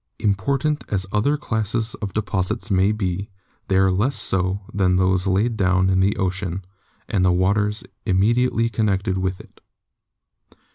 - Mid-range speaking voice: No, very low, 95 Hz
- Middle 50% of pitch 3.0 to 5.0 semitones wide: No, narrow, 2.6 semitones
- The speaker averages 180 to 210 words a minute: No, average, 150 wpm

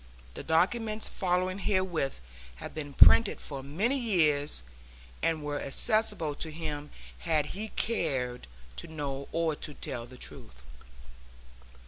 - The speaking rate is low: Yes, slow, 125 wpm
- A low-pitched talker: No, medium, 155 Hz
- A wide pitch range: No, average, 4.7 semitones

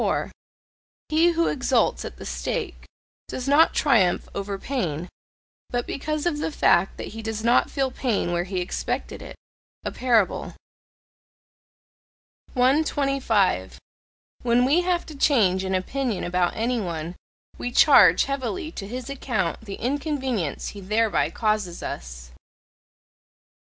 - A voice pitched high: Yes, high, 235 Hz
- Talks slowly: Yes, slow, 130 wpm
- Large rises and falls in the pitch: Yes, wide, 6.6 semitones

